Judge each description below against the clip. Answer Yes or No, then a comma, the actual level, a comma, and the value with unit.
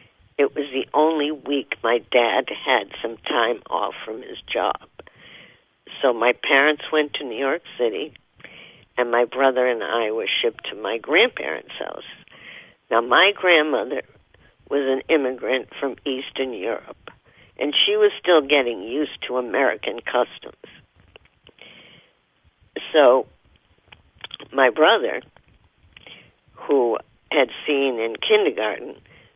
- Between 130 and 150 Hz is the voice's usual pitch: Yes, medium, 140 Hz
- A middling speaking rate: No, slow, 120 wpm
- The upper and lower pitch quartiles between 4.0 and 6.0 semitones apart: No, average, 3.6 semitones